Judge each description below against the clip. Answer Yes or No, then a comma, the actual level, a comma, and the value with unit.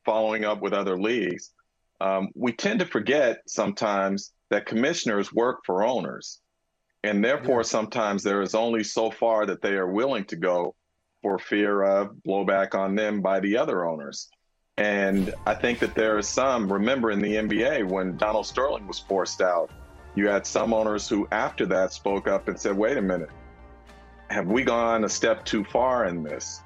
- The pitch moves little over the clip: Yes, narrow, 1.8 semitones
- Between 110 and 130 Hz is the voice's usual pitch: No, low, 100 Hz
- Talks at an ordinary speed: Yes, average, 180 wpm